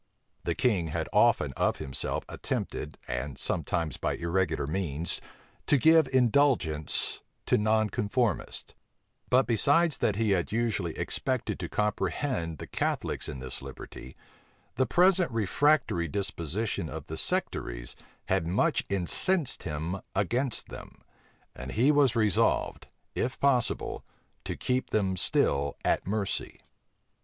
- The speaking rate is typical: No, slow, 125 wpm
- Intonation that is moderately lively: No, wide, 7.6 semitones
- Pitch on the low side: Yes, low, 105 Hz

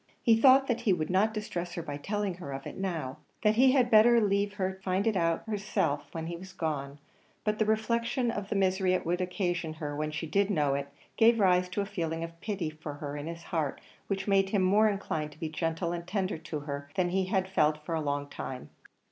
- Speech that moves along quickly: Yes, fast, 240 wpm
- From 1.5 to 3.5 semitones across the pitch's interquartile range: No, average, 4.6 semitones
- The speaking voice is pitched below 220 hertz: Yes, medium, 185 Hz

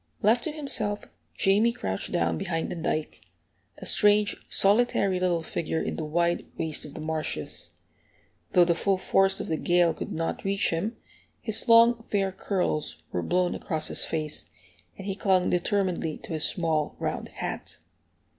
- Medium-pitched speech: Yes, medium, 180 Hz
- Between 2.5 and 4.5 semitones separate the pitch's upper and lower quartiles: Yes, average, 4.1 semitones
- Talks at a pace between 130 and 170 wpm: Yes, average, 165 wpm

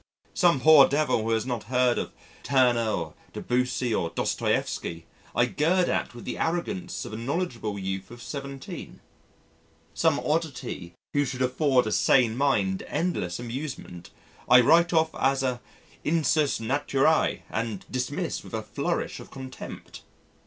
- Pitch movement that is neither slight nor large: Yes, average, 4.5 semitones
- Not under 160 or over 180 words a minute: No, average, 145 wpm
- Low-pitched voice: Yes, low, 130 Hz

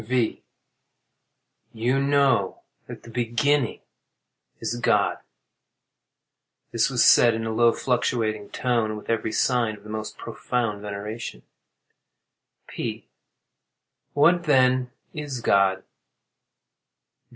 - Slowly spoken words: Yes, slow, 105 wpm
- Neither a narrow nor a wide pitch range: Yes, average, 3.0 semitones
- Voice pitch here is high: No, low, 115 Hz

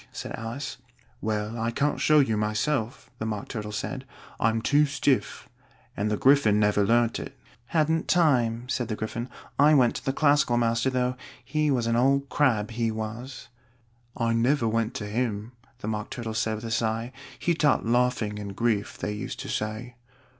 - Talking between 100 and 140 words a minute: No, average, 180 wpm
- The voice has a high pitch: No, low, 115 Hz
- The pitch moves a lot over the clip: No, average, 3.5 semitones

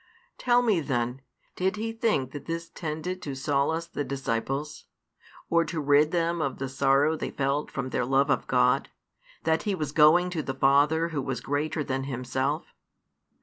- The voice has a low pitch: No, medium, 145 Hz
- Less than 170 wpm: No, average, 175 wpm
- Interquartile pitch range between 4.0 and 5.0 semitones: No, average, 3.6 semitones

